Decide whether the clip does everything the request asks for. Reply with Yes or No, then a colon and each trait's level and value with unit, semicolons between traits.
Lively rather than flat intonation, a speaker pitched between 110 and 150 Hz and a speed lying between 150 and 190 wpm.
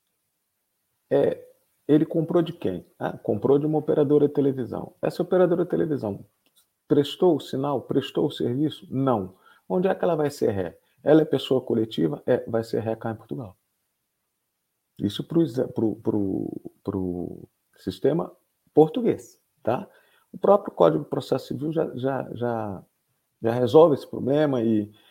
Yes: wide, 6.1 semitones; medium, 140 Hz; average, 155 wpm